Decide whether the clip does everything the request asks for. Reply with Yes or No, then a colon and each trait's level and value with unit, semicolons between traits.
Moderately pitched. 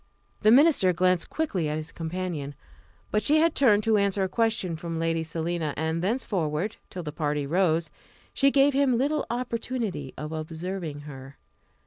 Yes: medium, 180 Hz